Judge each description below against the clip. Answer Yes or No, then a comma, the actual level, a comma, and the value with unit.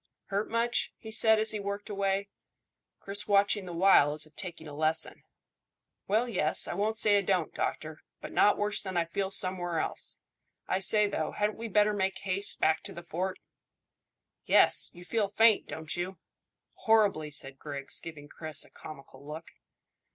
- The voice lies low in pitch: No, high, 190 Hz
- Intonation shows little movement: No, average, 4.5 semitones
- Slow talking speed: No, average, 175 wpm